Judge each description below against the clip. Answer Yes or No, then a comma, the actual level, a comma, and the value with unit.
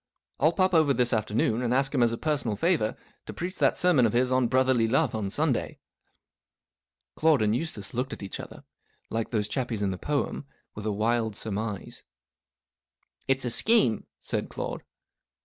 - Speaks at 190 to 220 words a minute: No, average, 180 wpm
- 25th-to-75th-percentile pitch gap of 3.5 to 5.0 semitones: Yes, average, 4.3 semitones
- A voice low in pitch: Yes, low, 120 Hz